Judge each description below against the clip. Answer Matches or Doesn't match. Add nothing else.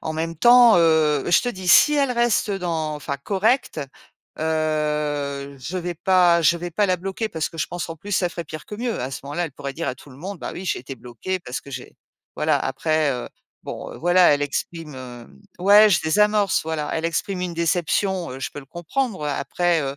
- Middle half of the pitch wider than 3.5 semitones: Matches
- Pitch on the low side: Doesn't match